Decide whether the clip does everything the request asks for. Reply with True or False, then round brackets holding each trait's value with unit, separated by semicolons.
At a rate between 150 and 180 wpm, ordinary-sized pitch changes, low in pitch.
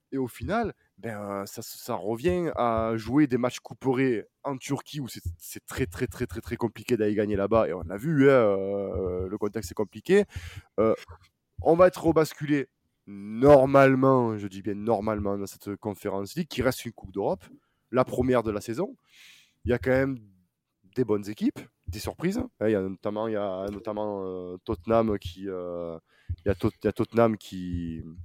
False (195 wpm; 4.4 semitones; 110 Hz)